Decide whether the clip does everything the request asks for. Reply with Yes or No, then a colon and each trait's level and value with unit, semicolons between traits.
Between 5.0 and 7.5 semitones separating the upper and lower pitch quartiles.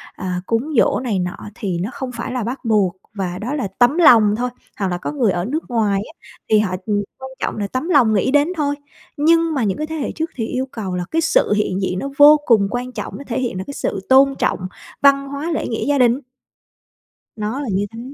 Yes: wide, 5.5 semitones